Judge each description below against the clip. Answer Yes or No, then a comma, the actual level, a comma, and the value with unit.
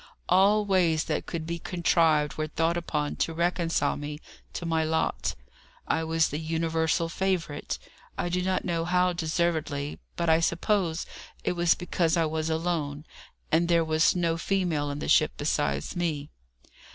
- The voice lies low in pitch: No, medium, 165 Hz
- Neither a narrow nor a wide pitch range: No, narrow, 1.7 semitones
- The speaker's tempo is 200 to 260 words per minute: No, average, 160 wpm